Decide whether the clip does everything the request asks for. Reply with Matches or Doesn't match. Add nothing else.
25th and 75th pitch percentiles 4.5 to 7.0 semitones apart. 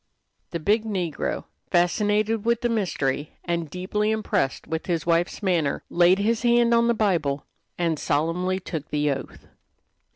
Matches